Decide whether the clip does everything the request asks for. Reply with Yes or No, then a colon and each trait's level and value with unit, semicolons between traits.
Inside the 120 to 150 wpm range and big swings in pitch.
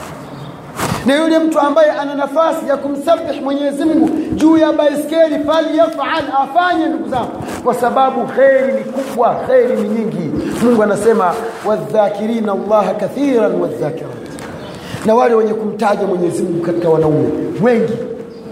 Yes: average, 125 wpm; wide, 5.7 semitones